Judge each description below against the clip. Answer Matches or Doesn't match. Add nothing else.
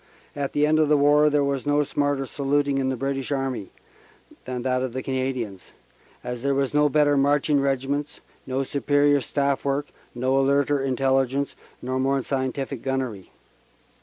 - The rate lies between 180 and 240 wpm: Doesn't match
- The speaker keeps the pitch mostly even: Matches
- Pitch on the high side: Doesn't match